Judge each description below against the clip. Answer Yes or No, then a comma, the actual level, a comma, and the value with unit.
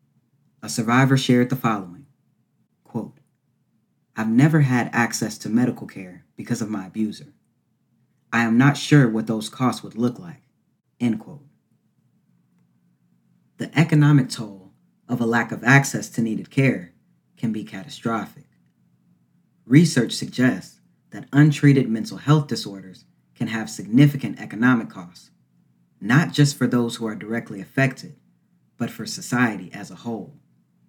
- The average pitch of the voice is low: Yes, low, 115 Hz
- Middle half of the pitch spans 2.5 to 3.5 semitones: No, average, 4.4 semitones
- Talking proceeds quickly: No, slow, 135 wpm